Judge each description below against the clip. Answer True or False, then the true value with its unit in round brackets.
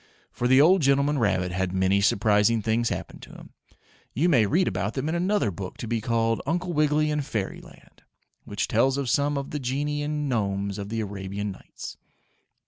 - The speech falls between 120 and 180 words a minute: False (190 wpm)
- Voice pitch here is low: True (120 Hz)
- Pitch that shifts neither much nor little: False (6.4 semitones)